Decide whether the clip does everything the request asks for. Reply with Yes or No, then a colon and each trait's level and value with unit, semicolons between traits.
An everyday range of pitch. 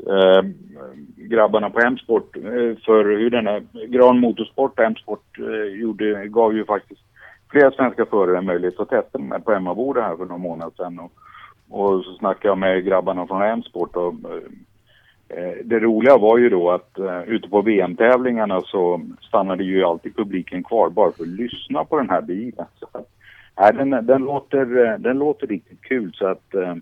Yes: average, 4.2 semitones